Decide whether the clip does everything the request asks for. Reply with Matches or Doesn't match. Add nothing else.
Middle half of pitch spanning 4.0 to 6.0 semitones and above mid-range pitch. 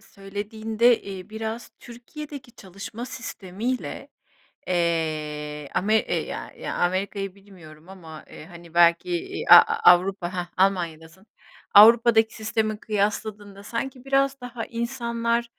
Matches